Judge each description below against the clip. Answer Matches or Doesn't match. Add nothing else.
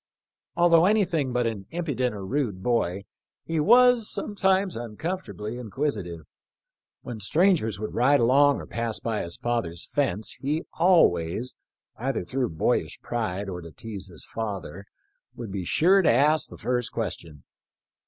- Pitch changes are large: Matches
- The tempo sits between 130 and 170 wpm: Matches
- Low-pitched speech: Matches